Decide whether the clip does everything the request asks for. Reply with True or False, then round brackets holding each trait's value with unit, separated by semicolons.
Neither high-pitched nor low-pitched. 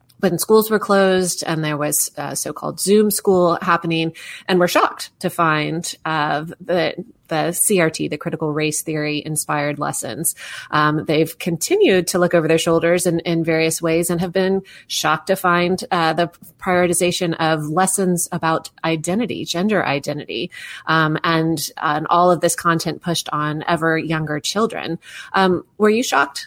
True (170 Hz)